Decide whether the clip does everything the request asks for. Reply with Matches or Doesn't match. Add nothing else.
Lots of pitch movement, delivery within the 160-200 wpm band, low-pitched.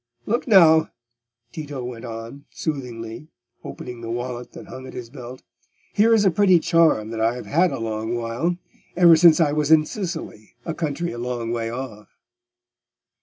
Matches